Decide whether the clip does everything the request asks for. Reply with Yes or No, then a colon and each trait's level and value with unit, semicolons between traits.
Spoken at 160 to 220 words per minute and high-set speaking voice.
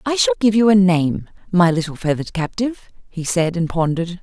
No: average, 200 wpm; medium, 180 Hz